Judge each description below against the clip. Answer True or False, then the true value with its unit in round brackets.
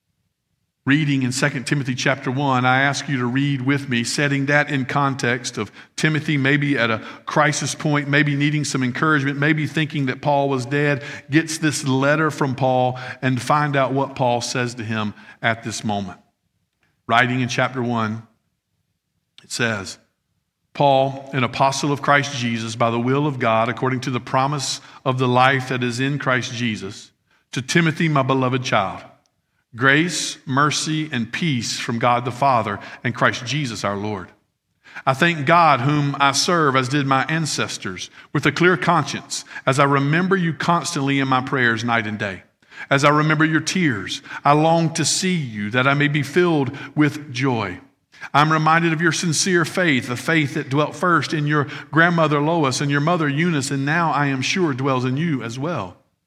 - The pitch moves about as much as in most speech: True (3.0 semitones)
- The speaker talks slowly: False (180 wpm)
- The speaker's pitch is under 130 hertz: False (140 Hz)